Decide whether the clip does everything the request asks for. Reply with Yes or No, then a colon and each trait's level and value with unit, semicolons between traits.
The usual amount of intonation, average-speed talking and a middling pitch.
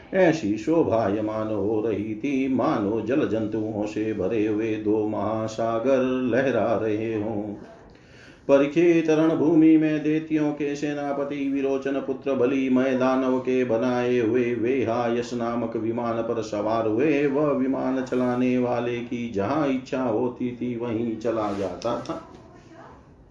No: average, 3.8 semitones; average, 125 wpm; low, 125 Hz